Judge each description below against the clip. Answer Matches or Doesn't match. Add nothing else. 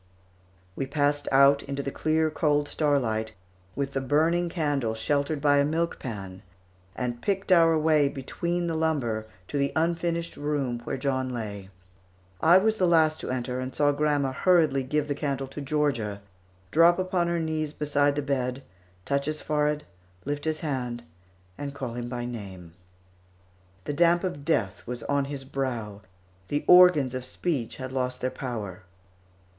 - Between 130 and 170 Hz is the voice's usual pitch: Matches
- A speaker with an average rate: Matches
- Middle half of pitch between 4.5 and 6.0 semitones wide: Doesn't match